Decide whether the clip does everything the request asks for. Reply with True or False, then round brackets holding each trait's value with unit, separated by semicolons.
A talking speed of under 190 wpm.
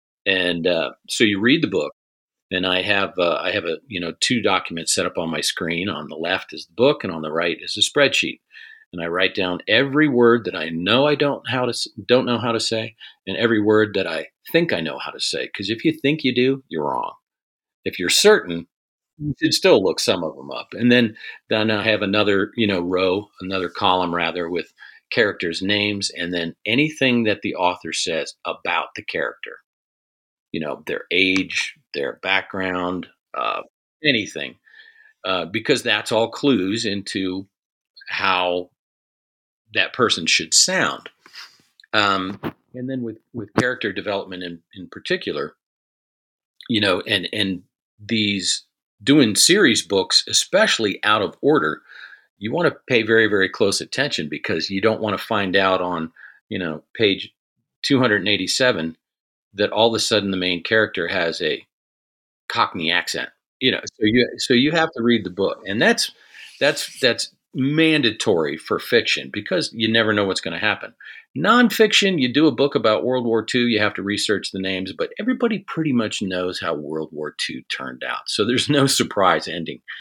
True (180 wpm)